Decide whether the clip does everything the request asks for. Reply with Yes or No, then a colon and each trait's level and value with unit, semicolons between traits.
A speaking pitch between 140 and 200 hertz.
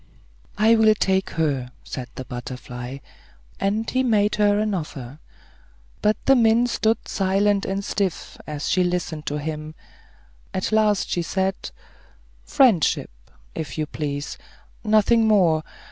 Yes: high, 190 Hz